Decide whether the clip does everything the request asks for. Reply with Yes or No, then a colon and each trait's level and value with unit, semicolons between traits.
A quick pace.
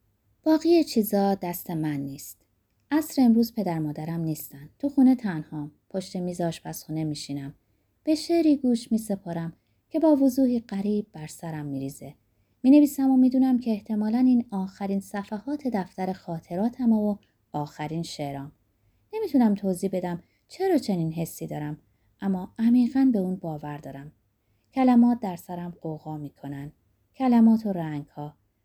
No: average, 135 wpm